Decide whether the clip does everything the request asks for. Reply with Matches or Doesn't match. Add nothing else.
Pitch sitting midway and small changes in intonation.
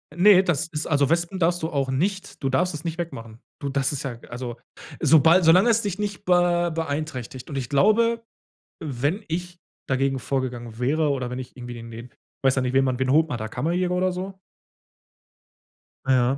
Doesn't match